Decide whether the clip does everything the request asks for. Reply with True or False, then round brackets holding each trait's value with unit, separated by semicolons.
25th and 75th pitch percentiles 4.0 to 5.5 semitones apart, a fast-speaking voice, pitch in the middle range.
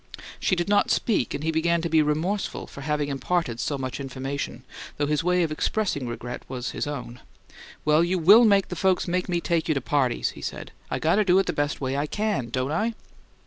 True (4.5 semitones; 225 wpm; 155 Hz)